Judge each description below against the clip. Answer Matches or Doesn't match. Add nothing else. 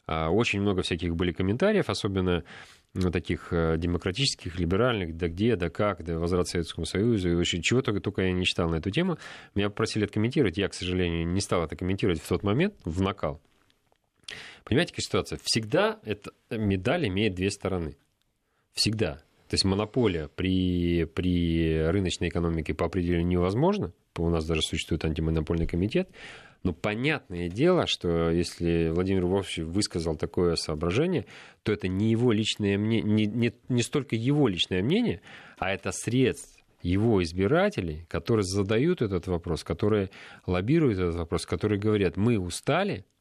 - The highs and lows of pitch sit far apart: Doesn't match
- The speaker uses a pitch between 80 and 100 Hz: Matches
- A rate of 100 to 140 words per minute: Doesn't match